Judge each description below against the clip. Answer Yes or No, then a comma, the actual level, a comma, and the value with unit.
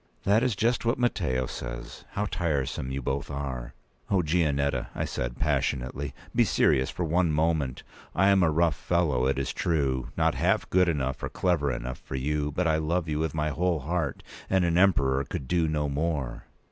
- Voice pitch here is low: Yes, very low, 75 Hz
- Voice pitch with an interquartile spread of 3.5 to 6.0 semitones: Yes, average, 4.5 semitones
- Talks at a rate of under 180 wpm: No, average, 185 wpm